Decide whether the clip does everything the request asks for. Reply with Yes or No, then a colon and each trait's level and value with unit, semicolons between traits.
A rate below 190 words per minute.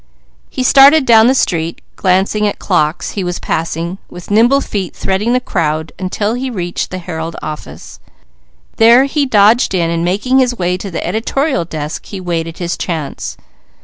Yes: average, 170 wpm